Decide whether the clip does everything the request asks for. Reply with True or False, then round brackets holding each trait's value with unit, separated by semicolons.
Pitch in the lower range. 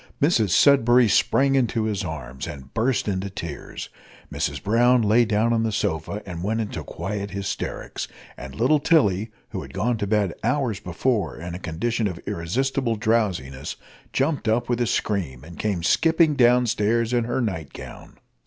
True (110 Hz)